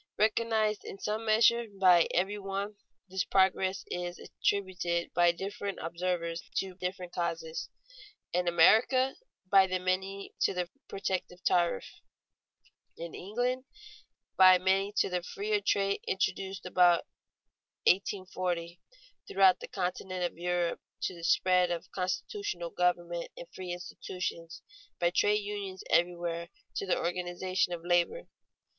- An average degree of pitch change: No, narrow, 2.1 semitones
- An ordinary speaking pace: No, slow, 125 wpm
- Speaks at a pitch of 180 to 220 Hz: Yes, medium, 185 Hz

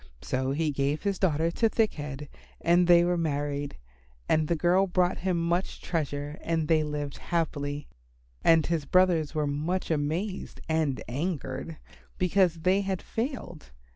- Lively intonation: No, average, 3.5 semitones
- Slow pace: No, average, 155 wpm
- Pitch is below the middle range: No, medium, 165 Hz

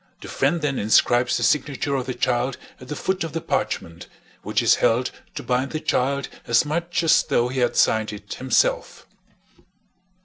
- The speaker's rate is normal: Yes, average, 180 wpm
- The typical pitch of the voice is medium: No, low, 130 Hz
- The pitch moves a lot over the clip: No, average, 4.0 semitones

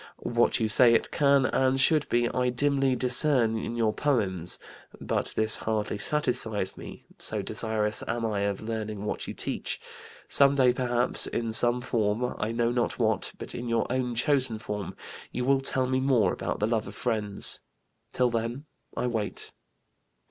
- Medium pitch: No, low, 120 Hz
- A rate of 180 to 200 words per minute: No, average, 170 wpm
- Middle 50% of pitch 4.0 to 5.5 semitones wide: No, average, 2.8 semitones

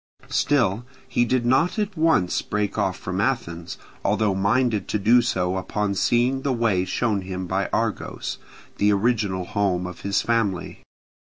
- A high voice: No, low, 105 Hz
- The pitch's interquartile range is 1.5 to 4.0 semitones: No, average, 4.4 semitones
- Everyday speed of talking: Yes, average, 155 wpm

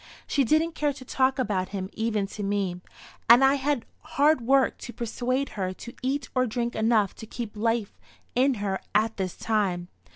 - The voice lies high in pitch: Yes, high, 230 Hz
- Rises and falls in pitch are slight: No, average, 4.5 semitones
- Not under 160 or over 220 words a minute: Yes, average, 185 wpm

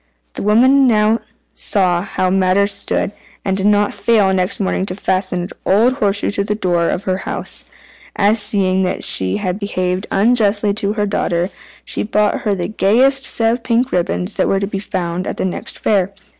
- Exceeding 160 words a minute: Yes, average, 190 wpm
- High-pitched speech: Yes, high, 200 Hz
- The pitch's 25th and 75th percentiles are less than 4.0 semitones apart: Yes, narrow, 2.4 semitones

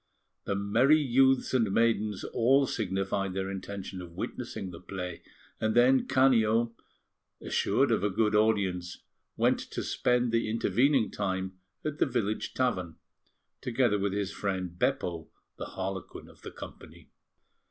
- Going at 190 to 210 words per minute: No, average, 140 wpm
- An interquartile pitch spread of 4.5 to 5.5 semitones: No, average, 4.1 semitones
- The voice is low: Yes, low, 105 Hz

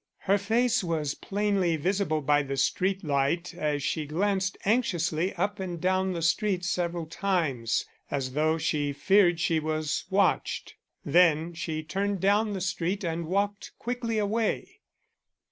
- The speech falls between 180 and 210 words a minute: No, average, 145 wpm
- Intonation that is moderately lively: Yes, average, 4.1 semitones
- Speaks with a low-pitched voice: No, medium, 175 Hz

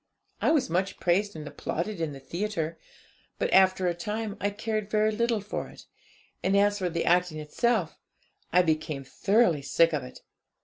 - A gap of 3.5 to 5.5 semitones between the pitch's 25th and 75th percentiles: Yes, average, 4.4 semitones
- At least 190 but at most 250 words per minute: No, average, 175 wpm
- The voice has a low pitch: No, medium, 185 Hz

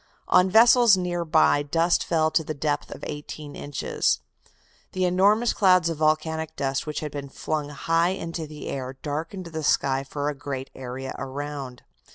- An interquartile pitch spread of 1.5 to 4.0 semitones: Yes, average, 3.1 semitones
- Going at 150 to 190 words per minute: Yes, average, 170 wpm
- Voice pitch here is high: No, medium, 155 Hz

